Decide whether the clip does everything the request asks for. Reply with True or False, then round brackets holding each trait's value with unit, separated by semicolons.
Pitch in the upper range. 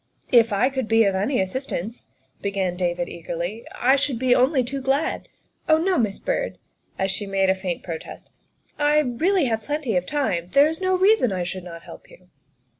True (230 Hz)